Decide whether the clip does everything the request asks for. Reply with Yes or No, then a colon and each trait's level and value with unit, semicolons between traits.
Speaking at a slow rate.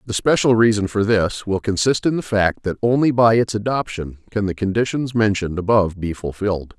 No: average, 195 wpm